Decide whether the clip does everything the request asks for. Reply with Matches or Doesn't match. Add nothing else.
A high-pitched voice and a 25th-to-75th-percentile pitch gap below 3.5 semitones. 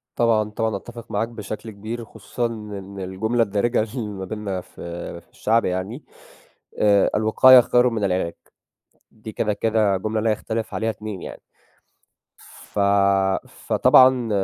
Doesn't match